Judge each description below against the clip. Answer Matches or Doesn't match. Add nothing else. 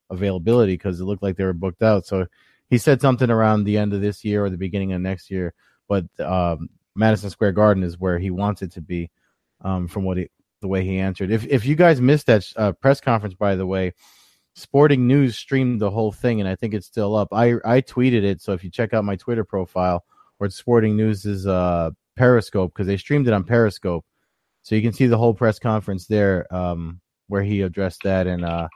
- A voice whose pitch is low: Matches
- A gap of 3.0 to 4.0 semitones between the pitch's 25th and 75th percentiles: Matches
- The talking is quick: Matches